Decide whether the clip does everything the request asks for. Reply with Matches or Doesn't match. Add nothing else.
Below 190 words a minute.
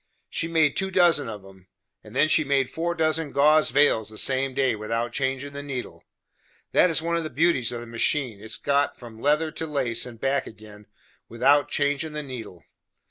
Doesn't match